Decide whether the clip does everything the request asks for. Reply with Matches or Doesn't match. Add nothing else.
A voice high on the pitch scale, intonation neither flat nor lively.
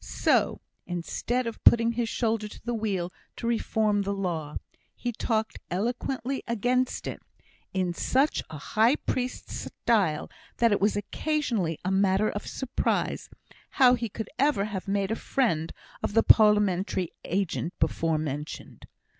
Matches